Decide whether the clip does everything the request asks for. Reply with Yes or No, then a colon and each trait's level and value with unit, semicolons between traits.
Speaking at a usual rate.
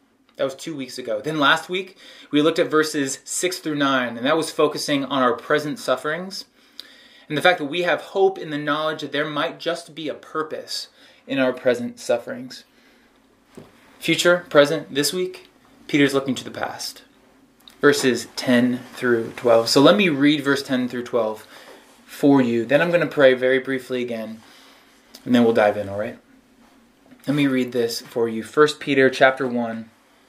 Yes: average, 180 wpm